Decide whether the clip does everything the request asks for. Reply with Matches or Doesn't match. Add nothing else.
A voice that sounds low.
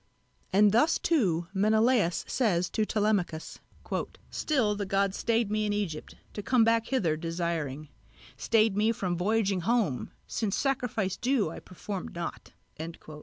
Doesn't match